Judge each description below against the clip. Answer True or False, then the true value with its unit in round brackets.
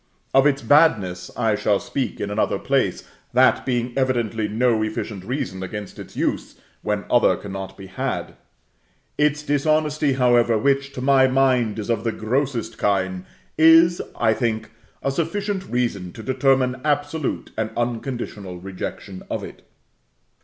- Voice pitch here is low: True (120 Hz)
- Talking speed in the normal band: True (145 wpm)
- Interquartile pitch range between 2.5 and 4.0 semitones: False (4.6 semitones)